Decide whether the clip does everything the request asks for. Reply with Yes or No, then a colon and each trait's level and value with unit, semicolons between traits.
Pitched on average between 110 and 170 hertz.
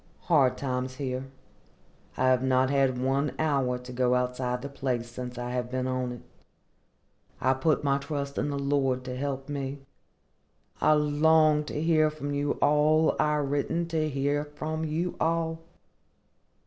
Yes: medium, 140 Hz